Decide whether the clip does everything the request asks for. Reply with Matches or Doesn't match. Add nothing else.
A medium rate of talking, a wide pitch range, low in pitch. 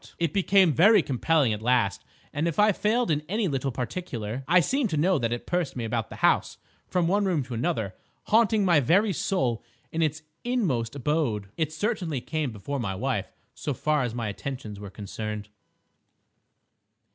Doesn't match